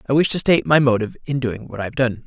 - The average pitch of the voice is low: Yes, low, 130 Hz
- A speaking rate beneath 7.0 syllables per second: No, 7.3 syllables/s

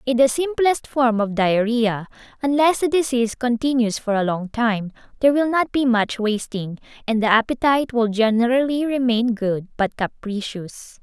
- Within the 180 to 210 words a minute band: No, average, 160 wpm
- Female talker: Yes, female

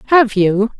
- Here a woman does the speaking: Yes, female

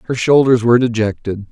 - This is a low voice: Yes, low, 120 Hz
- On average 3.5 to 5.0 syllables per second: No, 6.1 syllables/s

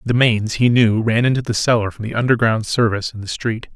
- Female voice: No, male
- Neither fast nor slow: No, fast, 240 wpm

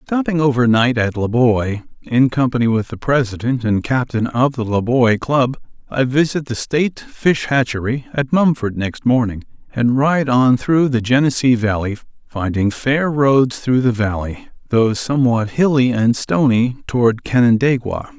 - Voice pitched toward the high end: No, low, 125 Hz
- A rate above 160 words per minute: No, average, 150 wpm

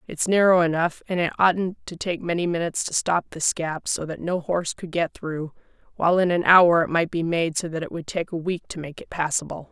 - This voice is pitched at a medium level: Yes, medium, 170 Hz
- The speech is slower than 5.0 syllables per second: No, 5.6 syllables/s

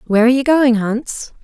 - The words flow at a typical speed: No, fast, 210 wpm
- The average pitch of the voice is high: Yes, high, 240 Hz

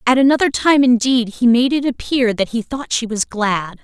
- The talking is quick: Yes, fast, 220 wpm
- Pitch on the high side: Yes, high, 245 Hz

